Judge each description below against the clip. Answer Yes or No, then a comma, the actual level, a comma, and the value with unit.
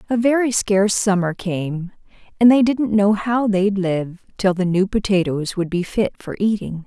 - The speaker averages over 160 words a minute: Yes, average, 185 wpm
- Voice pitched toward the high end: Yes, high, 200 Hz